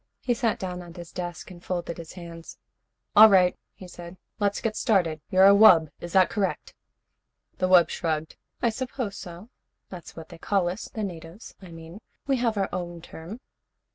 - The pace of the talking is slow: No, average, 185 wpm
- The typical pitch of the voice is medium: Yes, medium, 180 Hz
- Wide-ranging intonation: No, average, 3.2 semitones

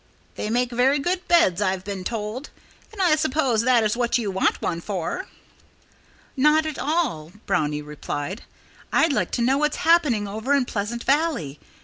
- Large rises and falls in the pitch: Yes, wide, 7.2 semitones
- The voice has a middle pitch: No, high, 240 Hz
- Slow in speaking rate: No, average, 165 wpm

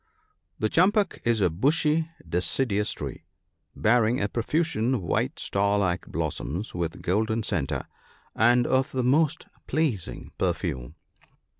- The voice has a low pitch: Yes, low, 110 Hz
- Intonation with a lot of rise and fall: Yes, wide, 6.3 semitones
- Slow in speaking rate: Yes, slow, 130 wpm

